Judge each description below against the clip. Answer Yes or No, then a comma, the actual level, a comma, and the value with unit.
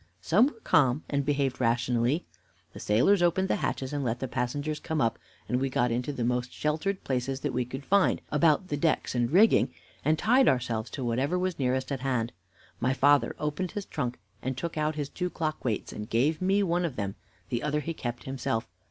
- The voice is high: No, medium, 140 Hz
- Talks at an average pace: No, fast, 210 wpm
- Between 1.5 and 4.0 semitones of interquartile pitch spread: No, average, 4.4 semitones